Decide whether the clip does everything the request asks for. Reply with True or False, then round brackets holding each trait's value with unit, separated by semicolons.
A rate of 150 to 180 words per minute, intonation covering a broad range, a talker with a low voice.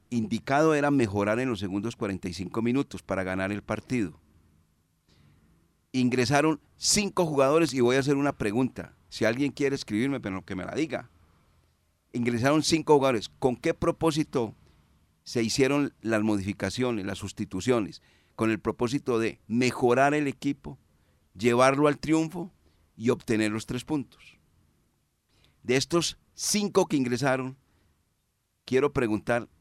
False (130 wpm; 6.4 semitones; 120 Hz)